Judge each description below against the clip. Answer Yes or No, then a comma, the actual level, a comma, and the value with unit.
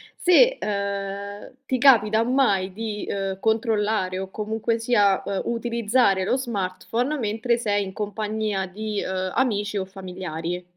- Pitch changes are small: No, average, 3.0 semitones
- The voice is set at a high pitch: Yes, high, 210 Hz